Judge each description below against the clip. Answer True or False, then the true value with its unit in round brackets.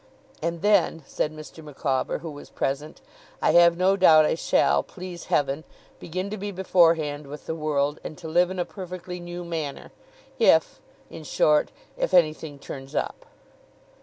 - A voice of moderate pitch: True (160 Hz)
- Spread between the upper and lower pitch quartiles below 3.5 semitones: True (3.0 semitones)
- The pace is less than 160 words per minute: False (165 wpm)